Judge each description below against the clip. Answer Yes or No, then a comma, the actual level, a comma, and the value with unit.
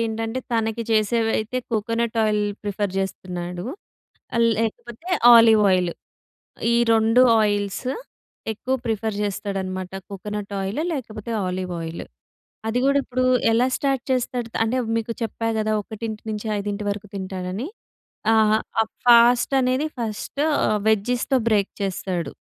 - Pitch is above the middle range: Yes, high, 220 Hz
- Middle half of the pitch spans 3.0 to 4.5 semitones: No, narrow, 2.6 semitones